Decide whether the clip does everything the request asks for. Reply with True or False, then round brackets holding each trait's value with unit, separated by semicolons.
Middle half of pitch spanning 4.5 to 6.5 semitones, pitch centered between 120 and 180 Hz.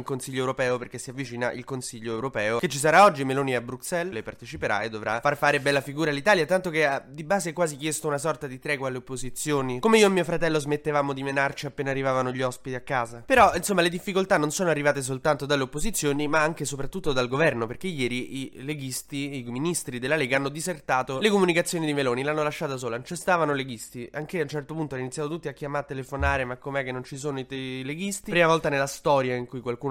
False (3.4 semitones; 140 Hz)